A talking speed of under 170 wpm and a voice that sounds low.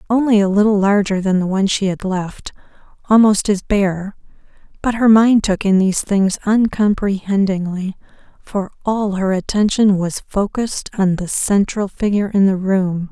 No: average, 155 wpm; high, 200 Hz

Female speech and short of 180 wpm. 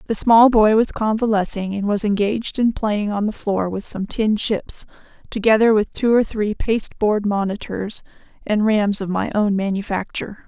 Yes: female; average, 170 wpm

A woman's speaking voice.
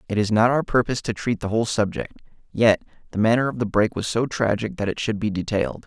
No: male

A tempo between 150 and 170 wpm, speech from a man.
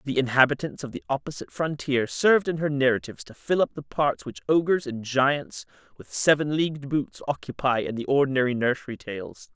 No: average, 180 wpm; male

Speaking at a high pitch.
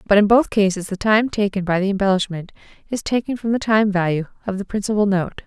Yes: high, 200 Hz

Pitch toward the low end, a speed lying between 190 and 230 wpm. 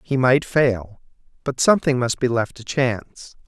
No: low, 125 Hz; average, 175 wpm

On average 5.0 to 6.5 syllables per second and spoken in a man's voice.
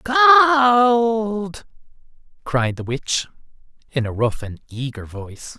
Yes: 5.4 syllables/s; male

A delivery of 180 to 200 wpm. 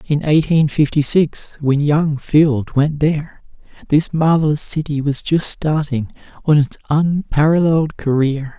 No: slow, 135 wpm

